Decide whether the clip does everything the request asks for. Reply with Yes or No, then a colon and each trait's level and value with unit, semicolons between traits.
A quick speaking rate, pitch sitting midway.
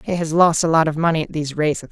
Yes: fast, 315 wpm; medium, 160 Hz